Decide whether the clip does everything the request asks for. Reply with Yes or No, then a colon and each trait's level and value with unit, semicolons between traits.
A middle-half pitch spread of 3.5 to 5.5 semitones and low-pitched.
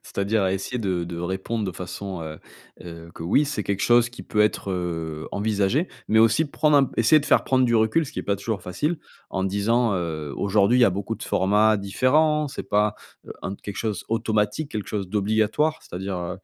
Yes: average, 3.8 semitones; low, 105 Hz